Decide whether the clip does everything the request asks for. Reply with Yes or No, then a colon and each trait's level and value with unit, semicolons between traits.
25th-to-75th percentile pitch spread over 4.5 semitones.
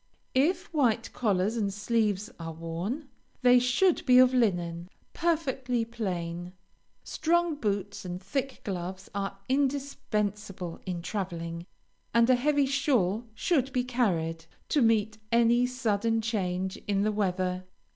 Yes: average, 5.3 semitones